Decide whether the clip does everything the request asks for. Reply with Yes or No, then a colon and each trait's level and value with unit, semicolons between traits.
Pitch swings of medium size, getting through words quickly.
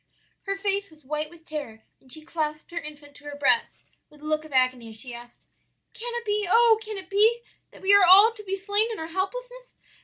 No: wide, 5.9 semitones; fast, 235 wpm